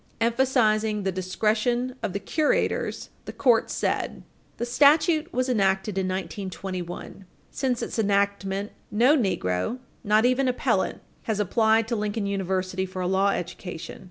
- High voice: Yes, high, 210 Hz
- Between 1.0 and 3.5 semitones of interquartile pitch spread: No, average, 4.0 semitones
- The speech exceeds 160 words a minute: No, slow, 135 wpm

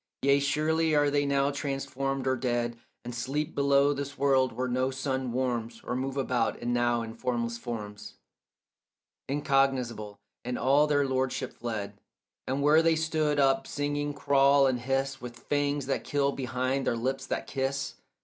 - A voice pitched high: No, low, 135 Hz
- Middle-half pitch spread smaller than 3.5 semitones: Yes, narrow, 2.4 semitones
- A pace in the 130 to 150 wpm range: No, average, 160 wpm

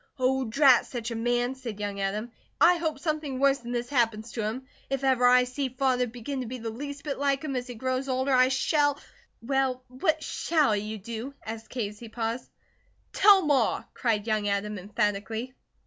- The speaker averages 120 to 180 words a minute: No, average, 200 wpm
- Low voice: No, very high, 250 Hz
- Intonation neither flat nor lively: Yes, average, 3.4 semitones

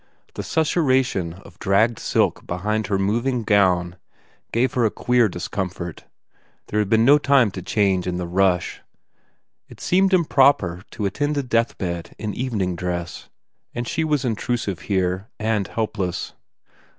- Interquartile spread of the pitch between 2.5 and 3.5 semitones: No, average, 5.3 semitones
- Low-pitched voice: Yes, low, 105 Hz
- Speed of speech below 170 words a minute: Yes, average, 150 wpm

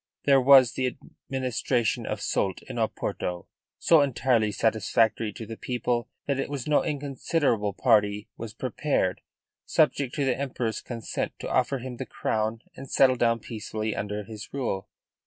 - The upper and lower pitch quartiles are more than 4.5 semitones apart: No, average, 3.6 semitones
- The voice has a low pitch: Yes, low, 120 Hz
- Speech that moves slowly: No, average, 155 wpm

